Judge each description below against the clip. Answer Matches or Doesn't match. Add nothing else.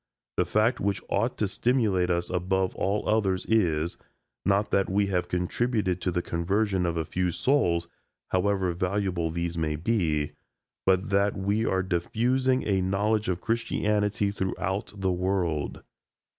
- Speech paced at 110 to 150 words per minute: Matches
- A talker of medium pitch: Doesn't match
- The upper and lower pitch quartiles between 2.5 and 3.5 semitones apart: Matches